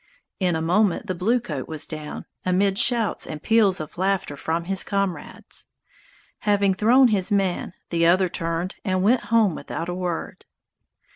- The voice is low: No, medium, 185 Hz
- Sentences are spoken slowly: No, average, 155 wpm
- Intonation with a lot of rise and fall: No, average, 3.5 semitones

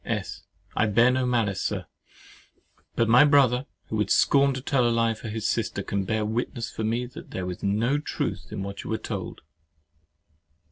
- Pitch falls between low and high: No, low, 115 Hz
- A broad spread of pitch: No, average, 2.9 semitones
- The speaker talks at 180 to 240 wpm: Yes, average, 190 wpm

